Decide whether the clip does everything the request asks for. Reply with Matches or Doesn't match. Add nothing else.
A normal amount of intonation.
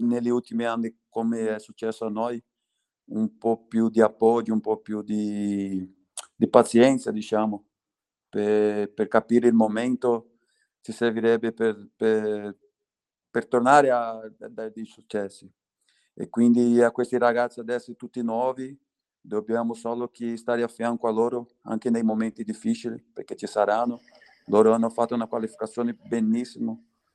Doesn't match